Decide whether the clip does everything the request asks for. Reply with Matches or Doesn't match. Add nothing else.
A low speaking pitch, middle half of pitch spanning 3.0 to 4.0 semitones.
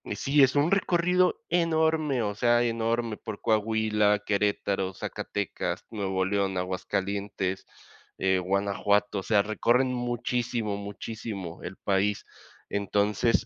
Matches